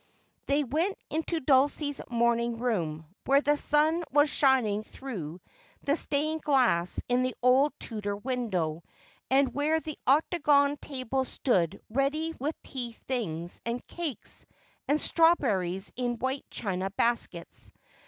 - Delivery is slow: Yes, slow, 125 wpm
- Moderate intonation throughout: Yes, average, 5.0 semitones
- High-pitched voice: Yes, very high, 260 Hz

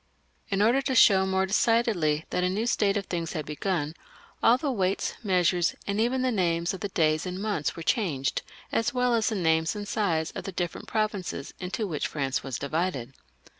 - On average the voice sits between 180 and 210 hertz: Yes, high, 190 Hz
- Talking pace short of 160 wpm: No, average, 200 wpm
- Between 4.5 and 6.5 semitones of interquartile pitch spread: Yes, average, 4.9 semitones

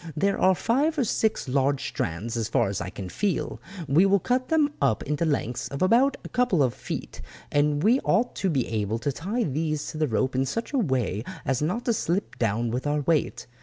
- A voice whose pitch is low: No, medium, 150 Hz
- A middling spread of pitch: No, wide, 8.7 semitones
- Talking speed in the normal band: No, fast, 220 wpm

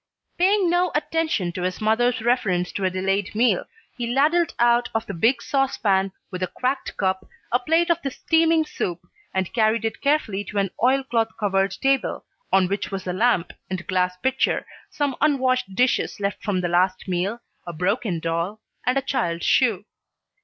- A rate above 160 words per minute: Yes, average, 175 wpm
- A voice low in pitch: No, high, 220 Hz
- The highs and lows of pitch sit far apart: Yes, wide, 5.9 semitones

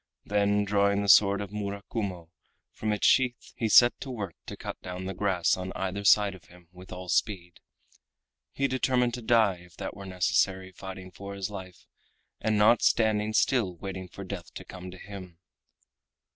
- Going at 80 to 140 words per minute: No, average, 180 wpm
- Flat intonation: Yes, narrow, 2.2 semitones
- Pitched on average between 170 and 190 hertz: No, low, 100 Hz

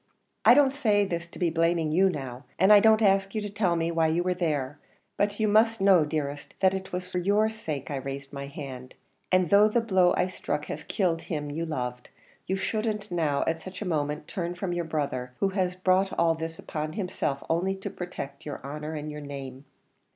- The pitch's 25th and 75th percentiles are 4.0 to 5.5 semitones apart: Yes, average, 4.5 semitones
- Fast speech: Yes, fast, 215 wpm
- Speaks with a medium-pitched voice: Yes, medium, 170 Hz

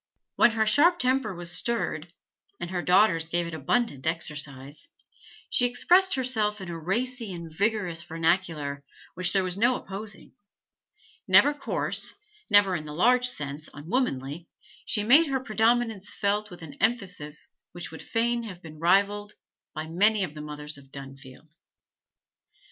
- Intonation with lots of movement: Yes, wide, 6.2 semitones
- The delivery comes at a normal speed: Yes, average, 150 wpm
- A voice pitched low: No, medium, 185 Hz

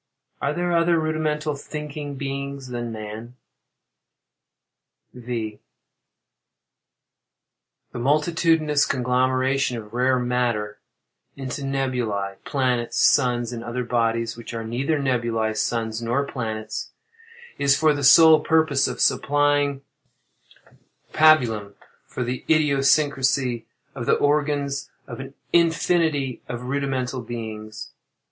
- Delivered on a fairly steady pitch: No, average, 3.6 semitones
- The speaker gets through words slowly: Yes, slow, 105 wpm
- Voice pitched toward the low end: Yes, low, 130 Hz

